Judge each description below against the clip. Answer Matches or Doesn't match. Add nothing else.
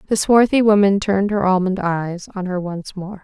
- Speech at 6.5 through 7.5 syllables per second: Doesn't match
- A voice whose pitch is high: Matches